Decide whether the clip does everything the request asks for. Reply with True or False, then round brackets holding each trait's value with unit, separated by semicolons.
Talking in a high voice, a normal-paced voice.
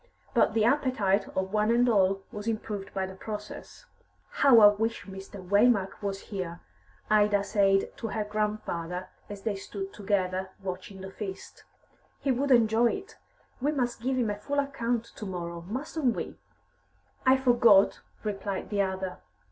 True (210 Hz; 155 wpm)